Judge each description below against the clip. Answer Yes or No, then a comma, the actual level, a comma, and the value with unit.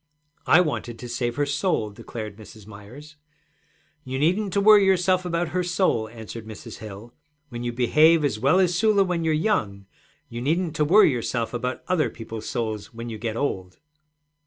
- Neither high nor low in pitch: No, low, 130 Hz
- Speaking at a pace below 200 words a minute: Yes, average, 180 wpm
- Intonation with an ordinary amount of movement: No, wide, 7.5 semitones